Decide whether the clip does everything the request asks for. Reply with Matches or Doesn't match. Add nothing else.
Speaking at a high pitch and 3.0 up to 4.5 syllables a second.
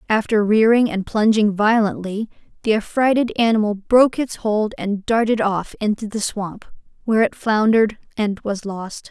Doesn't match